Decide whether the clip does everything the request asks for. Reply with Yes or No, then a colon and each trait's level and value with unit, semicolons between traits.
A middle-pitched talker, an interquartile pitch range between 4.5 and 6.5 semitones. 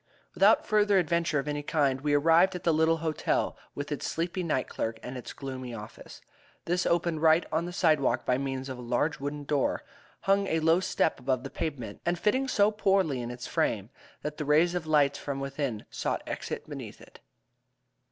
No: medium, 150 Hz; average, 4.0 semitones